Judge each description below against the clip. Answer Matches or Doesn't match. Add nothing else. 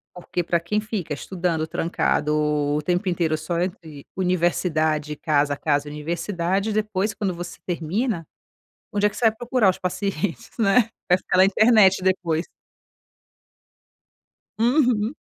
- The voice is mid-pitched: Matches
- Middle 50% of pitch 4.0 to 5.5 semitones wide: Matches